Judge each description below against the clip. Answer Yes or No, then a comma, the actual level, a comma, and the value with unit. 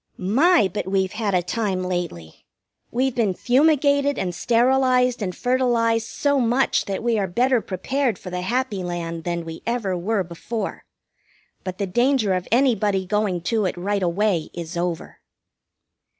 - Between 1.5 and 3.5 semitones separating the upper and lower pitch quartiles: No, average, 5.2 semitones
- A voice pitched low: No, high, 210 Hz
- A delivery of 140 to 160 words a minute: Yes, average, 155 wpm